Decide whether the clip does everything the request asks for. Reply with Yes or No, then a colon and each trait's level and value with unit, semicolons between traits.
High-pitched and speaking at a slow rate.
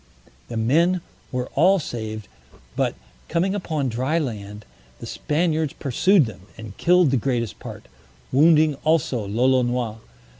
No: low, 130 Hz; slow, 125 wpm